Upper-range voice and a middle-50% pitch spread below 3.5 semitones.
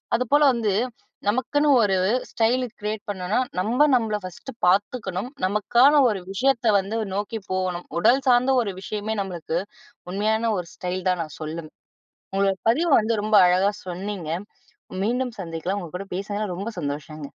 No: high, 205 Hz; average, 4.2 semitones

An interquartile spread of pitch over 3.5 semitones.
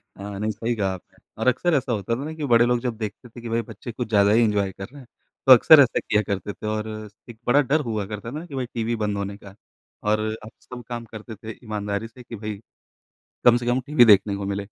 No: average, 2.9 semitones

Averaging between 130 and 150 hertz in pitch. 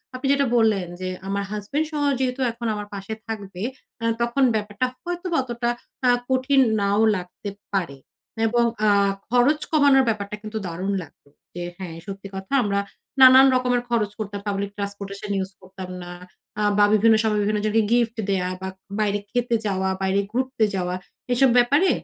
No: high, 210 Hz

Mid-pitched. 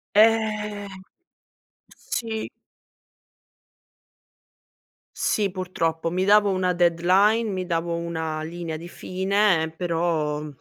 Yes: medium, 180 Hz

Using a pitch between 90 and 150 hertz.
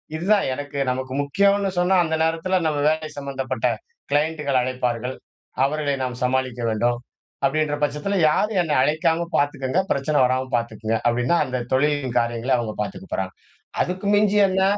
Yes: medium, 140 Hz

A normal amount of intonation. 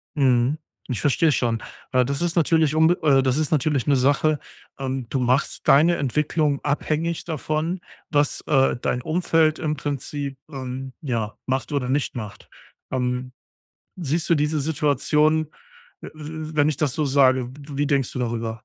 Yes: average, 3.0 semitones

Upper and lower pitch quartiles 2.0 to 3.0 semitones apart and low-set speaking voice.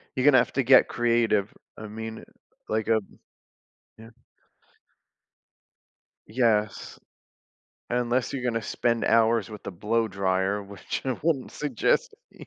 Yes: narrow, 2.6 semitones; low, 115 Hz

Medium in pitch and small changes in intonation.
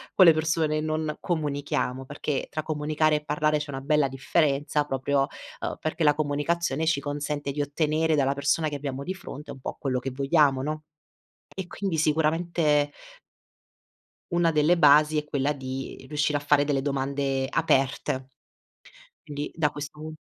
Yes: medium, 150 Hz; narrow, 1.9 semitones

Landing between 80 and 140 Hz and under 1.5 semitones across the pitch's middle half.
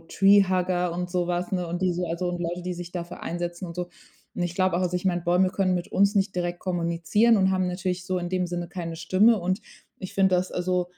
No: medium, 180 Hz; narrow, 1.1 semitones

